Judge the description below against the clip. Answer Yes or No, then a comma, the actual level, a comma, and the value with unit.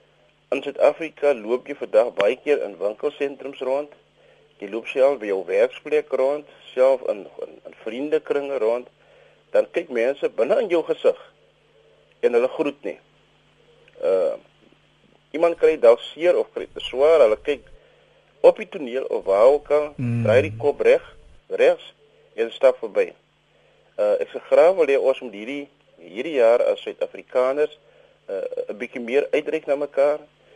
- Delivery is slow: No, average, 165 wpm